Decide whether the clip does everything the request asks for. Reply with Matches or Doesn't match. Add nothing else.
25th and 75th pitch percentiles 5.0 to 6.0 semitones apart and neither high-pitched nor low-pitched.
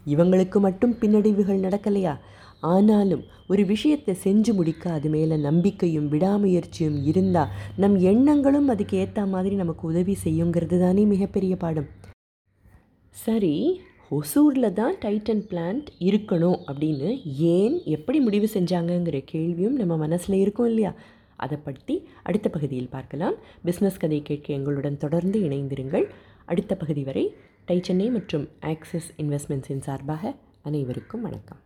Matches